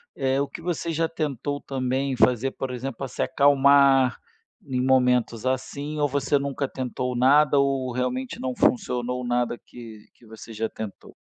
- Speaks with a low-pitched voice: Yes, low, 130 Hz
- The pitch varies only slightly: Yes, narrow, 2.1 semitones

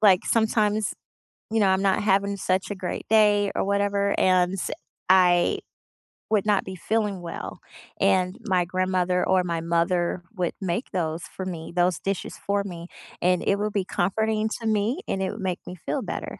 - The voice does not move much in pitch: Yes, narrow, 2.2 semitones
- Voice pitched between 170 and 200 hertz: Yes, high, 190 Hz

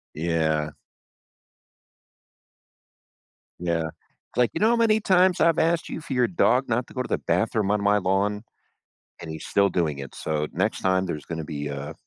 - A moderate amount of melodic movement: No, wide, 8.2 semitones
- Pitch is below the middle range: Yes, very low, 95 Hz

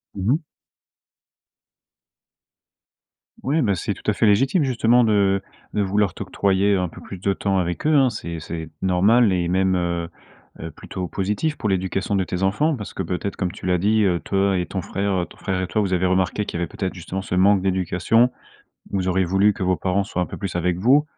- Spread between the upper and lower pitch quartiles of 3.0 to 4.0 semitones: No, narrow, 2.4 semitones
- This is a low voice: Yes, very low, 95 Hz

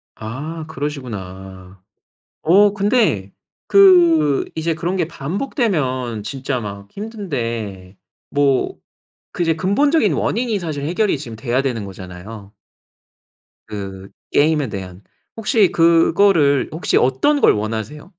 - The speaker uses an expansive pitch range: Yes, wide, 8.6 semitones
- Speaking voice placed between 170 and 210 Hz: No, medium, 145 Hz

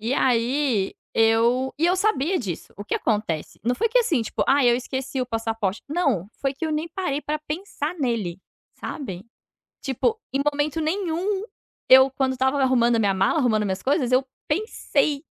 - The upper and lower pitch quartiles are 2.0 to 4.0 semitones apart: No, average, 5.2 semitones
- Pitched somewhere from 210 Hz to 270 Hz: Yes, very high, 265 Hz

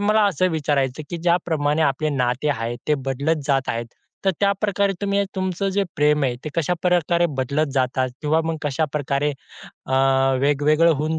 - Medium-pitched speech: Yes, medium, 150 Hz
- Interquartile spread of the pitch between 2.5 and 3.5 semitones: No, average, 4.0 semitones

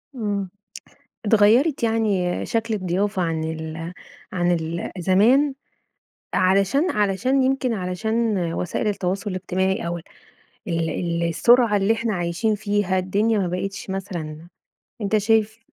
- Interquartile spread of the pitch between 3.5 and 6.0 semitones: Yes, average, 3.8 semitones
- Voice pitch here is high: Yes, high, 195 Hz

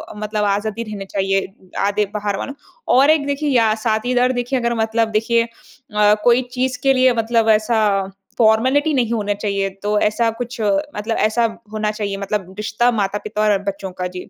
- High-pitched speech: Yes, high, 220 Hz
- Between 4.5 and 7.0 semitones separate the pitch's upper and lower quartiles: No, average, 2.9 semitones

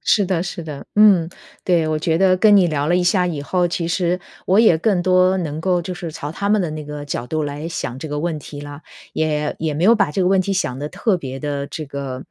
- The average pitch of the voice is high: No, medium, 165 Hz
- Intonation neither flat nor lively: Yes, average, 3.7 semitones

